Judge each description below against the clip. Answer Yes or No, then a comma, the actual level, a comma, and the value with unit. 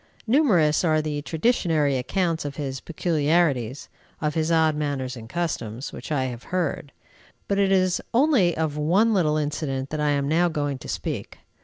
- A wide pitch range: No, average, 3.5 semitones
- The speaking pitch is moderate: Yes, medium, 155 Hz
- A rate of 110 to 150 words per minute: No, average, 170 wpm